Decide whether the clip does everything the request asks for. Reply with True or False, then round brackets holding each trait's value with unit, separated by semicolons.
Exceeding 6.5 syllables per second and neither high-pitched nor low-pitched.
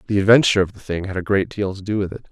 False (7.6 syllables/s; 100 Hz)